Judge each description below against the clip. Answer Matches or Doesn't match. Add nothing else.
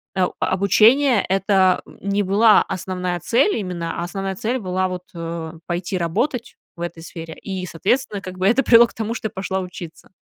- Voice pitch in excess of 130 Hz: Matches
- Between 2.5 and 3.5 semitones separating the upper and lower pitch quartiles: Matches